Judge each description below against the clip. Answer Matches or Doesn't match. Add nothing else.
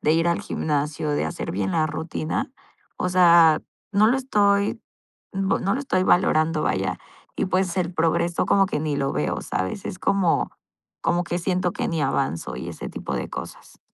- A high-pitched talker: Doesn't match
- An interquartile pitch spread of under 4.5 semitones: Matches